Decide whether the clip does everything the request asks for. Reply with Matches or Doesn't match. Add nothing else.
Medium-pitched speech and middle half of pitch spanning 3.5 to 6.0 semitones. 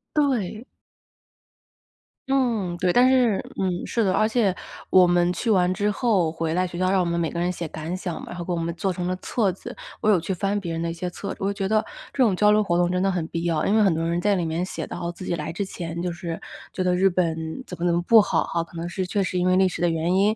Doesn't match